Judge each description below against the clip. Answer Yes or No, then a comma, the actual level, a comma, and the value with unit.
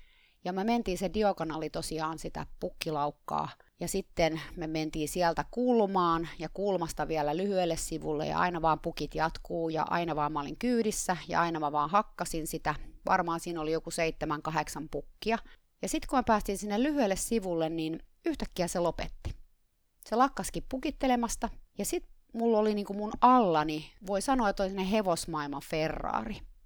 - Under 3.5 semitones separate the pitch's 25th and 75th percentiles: No, average, 5.1 semitones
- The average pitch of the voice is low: No, medium, 170 Hz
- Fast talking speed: Yes, fast, 160 wpm